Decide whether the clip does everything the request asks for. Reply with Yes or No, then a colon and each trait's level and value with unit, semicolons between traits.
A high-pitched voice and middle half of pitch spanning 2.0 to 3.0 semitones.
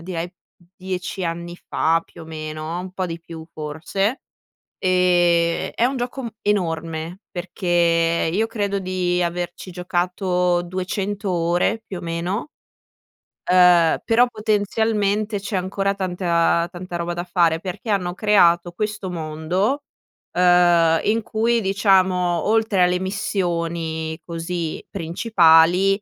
No: medium, 180 Hz; average, 2.7 semitones